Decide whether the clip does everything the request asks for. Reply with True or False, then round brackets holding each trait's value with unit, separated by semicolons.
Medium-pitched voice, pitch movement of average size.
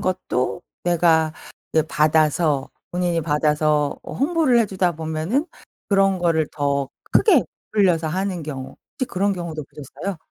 True (165 Hz; 3.9 semitones)